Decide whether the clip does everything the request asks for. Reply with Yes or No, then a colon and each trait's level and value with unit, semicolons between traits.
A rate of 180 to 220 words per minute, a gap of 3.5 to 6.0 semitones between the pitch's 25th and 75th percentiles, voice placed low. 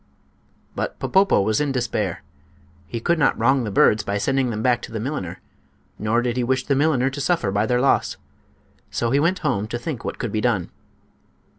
Yes: average, 200 wpm; average, 4.1 semitones; low, 125 Hz